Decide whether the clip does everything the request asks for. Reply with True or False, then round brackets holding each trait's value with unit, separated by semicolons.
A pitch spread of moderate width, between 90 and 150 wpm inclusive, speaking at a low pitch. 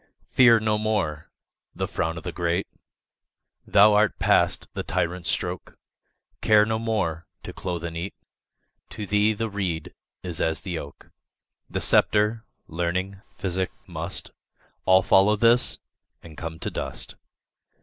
True (3.9 semitones; 140 wpm; 95 Hz)